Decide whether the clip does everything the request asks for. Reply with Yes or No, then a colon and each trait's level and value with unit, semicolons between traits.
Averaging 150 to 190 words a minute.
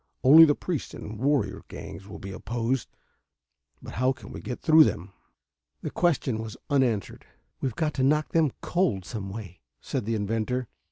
Yes: average, 170 wpm